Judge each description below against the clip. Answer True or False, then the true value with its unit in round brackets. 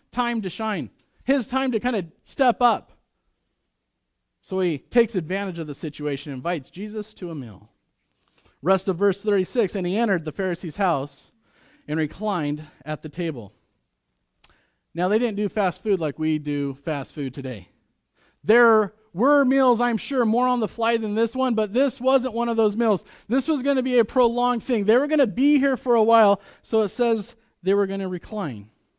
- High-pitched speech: True (210 Hz)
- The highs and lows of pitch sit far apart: True (6.2 semitones)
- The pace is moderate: True (195 wpm)